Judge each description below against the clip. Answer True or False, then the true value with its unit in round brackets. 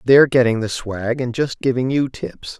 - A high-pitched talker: False (125 Hz)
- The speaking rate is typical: False (210 wpm)